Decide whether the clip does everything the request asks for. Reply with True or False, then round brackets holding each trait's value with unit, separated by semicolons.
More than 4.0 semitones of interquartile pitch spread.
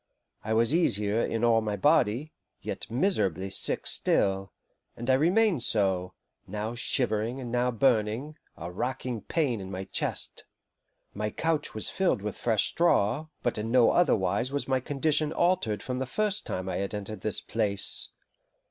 True (5.0 semitones)